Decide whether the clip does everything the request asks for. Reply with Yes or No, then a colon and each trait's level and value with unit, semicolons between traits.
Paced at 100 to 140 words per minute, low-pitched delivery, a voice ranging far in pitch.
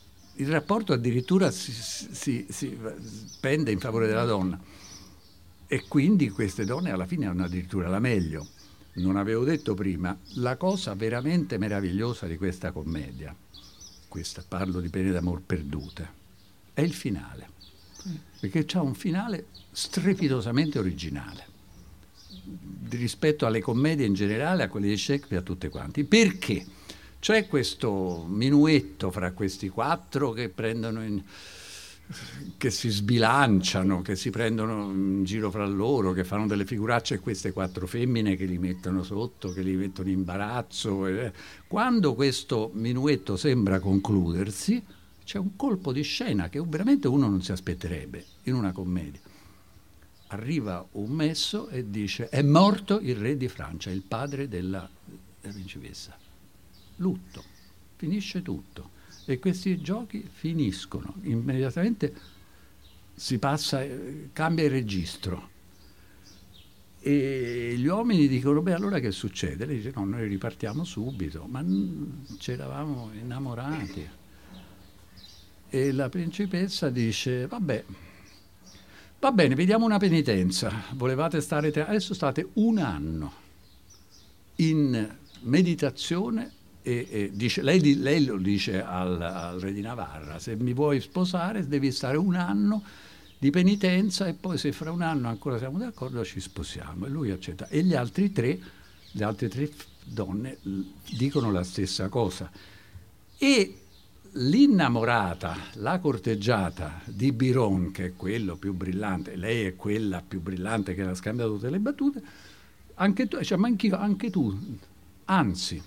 Yes: average, 135 wpm; low, 105 Hz; wide, 7.2 semitones